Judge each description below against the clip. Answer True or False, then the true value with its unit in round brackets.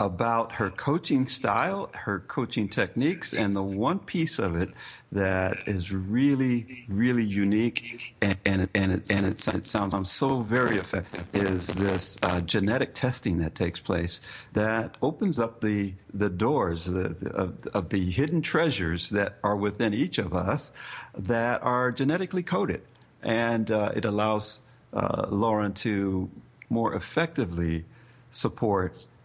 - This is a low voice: True (105 Hz)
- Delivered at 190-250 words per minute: False (145 wpm)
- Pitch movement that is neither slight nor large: True (3.7 semitones)